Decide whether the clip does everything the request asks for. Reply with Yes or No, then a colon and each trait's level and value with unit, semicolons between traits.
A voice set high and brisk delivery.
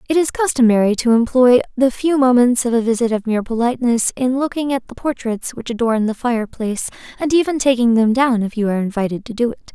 Yes: high, 240 Hz; fast, 215 wpm